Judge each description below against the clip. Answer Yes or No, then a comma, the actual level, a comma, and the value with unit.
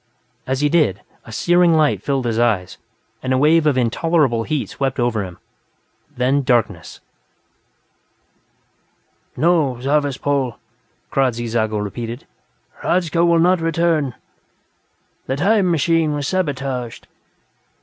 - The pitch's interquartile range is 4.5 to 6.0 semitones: Yes, average, 5.3 semitones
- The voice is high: No, medium, 140 Hz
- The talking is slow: Yes, slow, 120 wpm